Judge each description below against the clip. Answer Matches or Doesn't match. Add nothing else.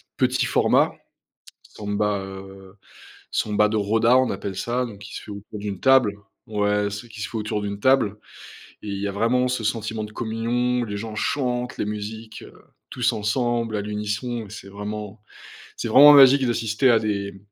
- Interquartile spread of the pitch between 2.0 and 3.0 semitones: Matches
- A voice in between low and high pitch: Doesn't match